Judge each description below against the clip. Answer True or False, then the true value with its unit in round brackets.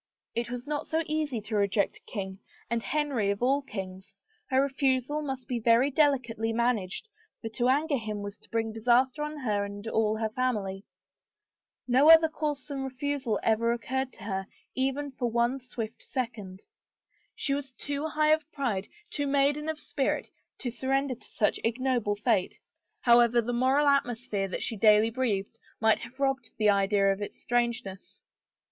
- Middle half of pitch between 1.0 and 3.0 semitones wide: False (4.1 semitones)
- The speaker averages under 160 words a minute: False (170 wpm)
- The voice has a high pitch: True (240 Hz)